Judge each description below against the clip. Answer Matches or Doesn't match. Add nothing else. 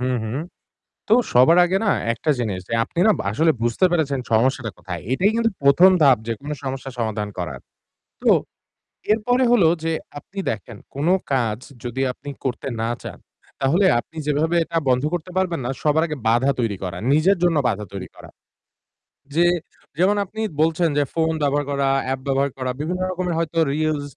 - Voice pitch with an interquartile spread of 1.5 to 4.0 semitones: Doesn't match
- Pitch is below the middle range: Doesn't match